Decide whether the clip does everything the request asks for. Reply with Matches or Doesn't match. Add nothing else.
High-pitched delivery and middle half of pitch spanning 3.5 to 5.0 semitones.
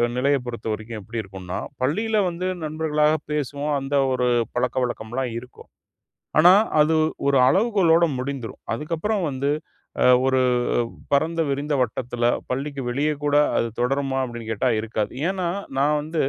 Doesn't match